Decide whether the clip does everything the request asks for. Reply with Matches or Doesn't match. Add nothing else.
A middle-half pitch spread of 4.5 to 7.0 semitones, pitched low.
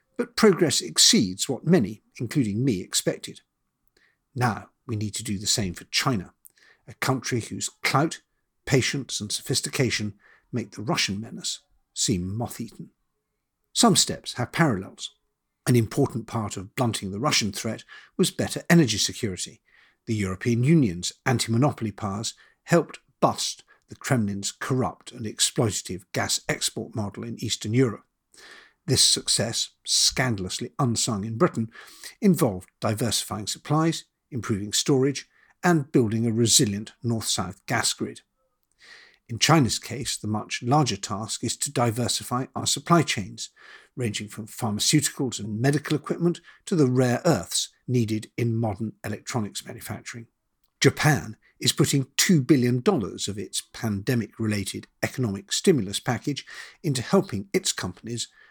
Matches